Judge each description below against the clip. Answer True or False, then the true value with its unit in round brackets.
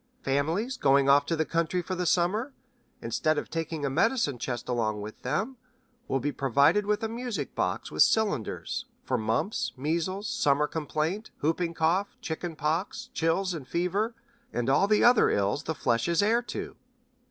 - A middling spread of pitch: False (6.1 semitones)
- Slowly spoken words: False (170 wpm)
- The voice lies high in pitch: False (165 Hz)